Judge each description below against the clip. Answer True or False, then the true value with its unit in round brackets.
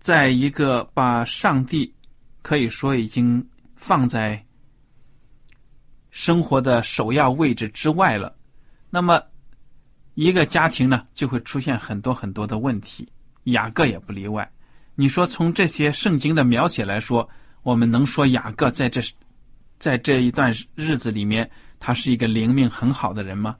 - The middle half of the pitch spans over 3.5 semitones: False (3.2 semitones)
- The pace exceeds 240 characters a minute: False (220 characters per minute)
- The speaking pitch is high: False (130 Hz)